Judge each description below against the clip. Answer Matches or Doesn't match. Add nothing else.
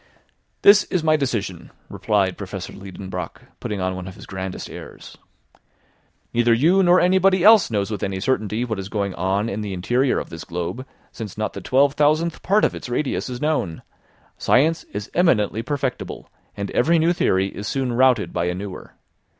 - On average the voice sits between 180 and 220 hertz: Doesn't match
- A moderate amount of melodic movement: Doesn't match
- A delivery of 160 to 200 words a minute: Matches